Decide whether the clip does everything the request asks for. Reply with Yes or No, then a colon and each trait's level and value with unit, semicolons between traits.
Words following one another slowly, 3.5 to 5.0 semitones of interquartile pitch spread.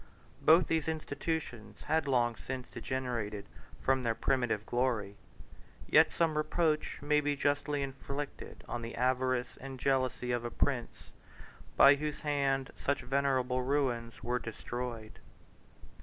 No: slow, 125 wpm; average, 3.0 semitones